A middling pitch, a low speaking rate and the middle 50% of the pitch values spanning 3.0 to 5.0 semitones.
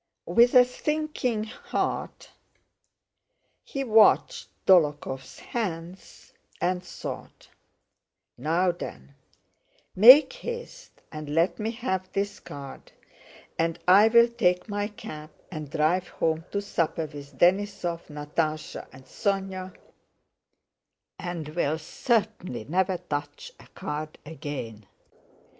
No: medium, 180 Hz; slow, 100 wpm; wide, 5.6 semitones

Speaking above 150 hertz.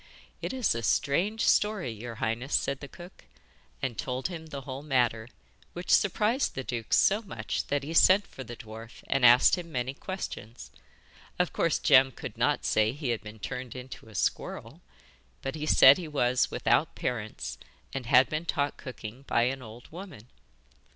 No: low, 130 Hz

